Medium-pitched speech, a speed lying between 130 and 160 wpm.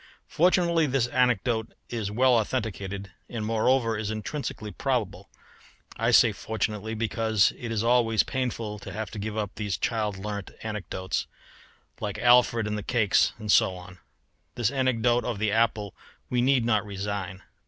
No: low, 110 Hz; average, 155 wpm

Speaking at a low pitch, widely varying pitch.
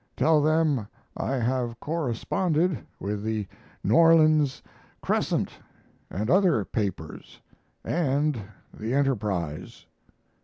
Yes: low, 130 Hz; wide, 6.4 semitones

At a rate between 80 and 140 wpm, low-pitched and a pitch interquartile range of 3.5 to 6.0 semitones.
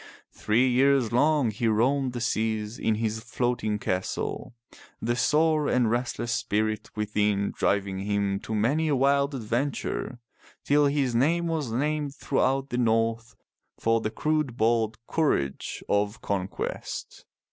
Yes: slow, 135 wpm; low, 120 Hz; average, 4.3 semitones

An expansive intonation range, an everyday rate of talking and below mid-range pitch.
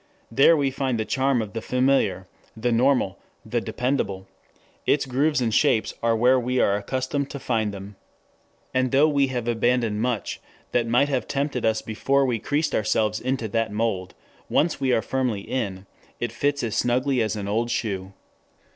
No: average, 3.6 semitones; average, 175 wpm; low, 120 Hz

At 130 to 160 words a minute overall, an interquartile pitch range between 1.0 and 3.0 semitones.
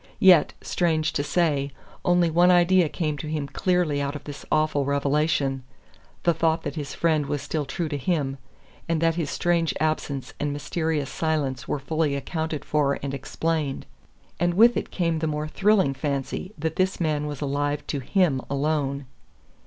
No: average, 175 wpm; average, 2.7 semitones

